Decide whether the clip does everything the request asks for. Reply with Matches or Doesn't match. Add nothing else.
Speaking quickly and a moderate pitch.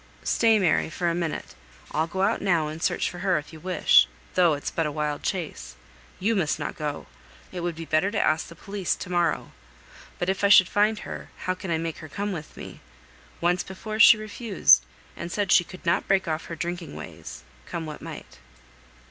Matches